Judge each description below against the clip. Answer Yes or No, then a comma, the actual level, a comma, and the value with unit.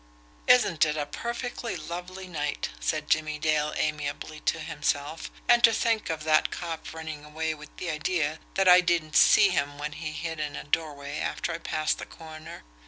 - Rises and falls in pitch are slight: Yes, narrow, 2.2 semitones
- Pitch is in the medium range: Yes, medium, 155 Hz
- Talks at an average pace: Yes, average, 180 wpm